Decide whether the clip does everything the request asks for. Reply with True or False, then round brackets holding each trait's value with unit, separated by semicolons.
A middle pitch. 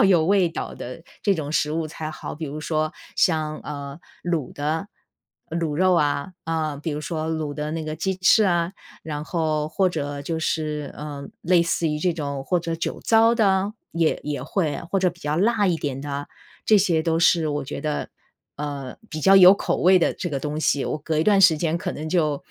True (160 Hz)